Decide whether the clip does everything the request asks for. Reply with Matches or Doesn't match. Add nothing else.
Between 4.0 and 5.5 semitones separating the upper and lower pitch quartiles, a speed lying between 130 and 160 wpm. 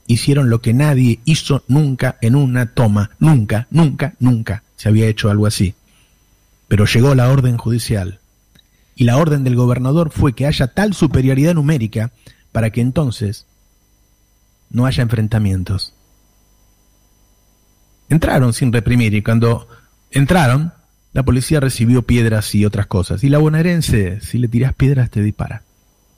Matches